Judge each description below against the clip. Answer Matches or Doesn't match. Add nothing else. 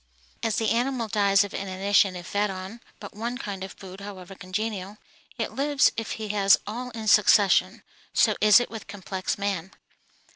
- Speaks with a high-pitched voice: Matches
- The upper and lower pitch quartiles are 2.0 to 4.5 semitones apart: Matches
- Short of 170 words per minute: Doesn't match